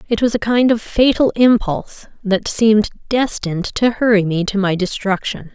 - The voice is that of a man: No, female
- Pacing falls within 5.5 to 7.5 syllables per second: No, 5.0 syllables/s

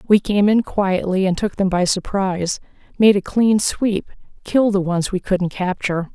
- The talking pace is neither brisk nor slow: Yes, average, 175 wpm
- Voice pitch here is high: Yes, high, 195 Hz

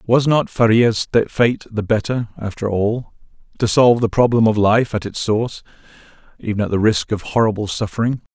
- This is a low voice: Yes, low, 110 Hz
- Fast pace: No, average, 165 wpm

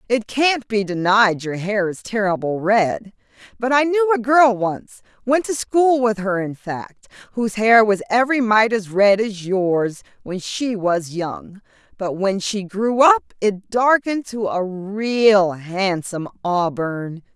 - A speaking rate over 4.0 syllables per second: No, 3.8 syllables/s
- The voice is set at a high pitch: Yes, high, 210 Hz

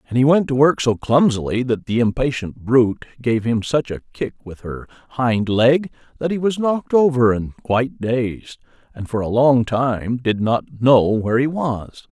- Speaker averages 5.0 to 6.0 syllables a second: No, 4.6 syllables/s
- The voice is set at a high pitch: No, low, 125 Hz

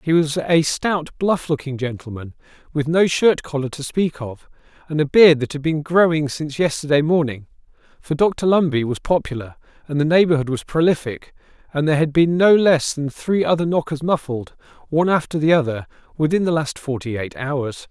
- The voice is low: No, medium, 150 Hz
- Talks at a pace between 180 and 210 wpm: Yes, average, 185 wpm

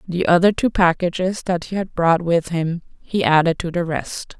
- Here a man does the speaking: No, female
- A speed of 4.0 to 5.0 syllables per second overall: Yes, 4.7 syllables/s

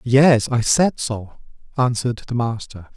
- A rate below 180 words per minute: Yes, average, 140 wpm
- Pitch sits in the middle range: No, low, 120 Hz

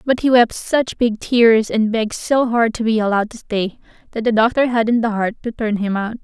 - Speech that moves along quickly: Yes, fast, 240 wpm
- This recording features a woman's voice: Yes, female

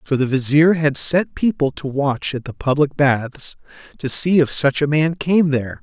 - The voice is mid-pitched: Yes, medium, 145 Hz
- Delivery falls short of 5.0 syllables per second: Yes, 4.6 syllables/s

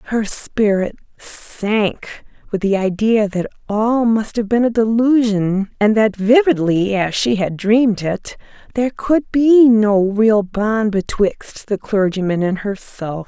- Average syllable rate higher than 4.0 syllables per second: No, 3.8 syllables/s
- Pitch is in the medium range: No, high, 215 Hz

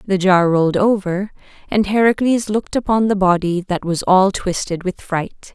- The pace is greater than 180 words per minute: No, average, 175 wpm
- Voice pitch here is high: Yes, high, 195 Hz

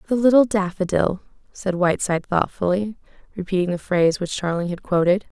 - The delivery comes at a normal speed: Yes, average, 145 wpm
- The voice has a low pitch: No, high, 190 Hz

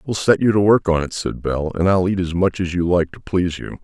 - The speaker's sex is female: No, male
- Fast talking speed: Yes, fast, 315 wpm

